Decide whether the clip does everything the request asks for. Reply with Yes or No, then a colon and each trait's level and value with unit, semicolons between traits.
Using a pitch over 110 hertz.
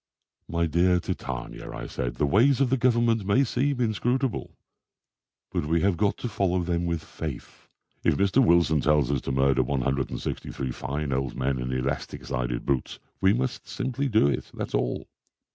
No: very low, 85 Hz